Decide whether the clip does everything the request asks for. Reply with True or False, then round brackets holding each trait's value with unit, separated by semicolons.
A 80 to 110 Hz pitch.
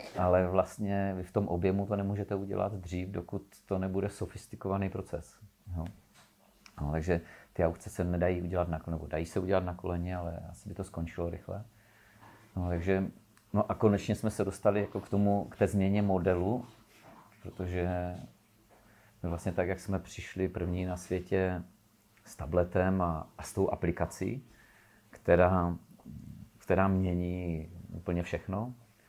True (95 Hz)